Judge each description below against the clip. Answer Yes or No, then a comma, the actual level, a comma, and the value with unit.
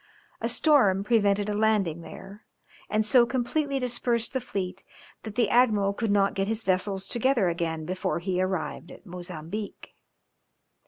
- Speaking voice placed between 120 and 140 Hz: No, high, 205 Hz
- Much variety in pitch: No, average, 4.0 semitones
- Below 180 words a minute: Yes, average, 150 wpm